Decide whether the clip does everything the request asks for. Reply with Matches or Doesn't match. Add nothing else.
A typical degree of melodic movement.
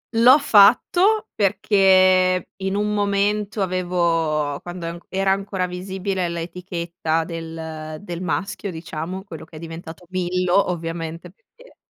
Matches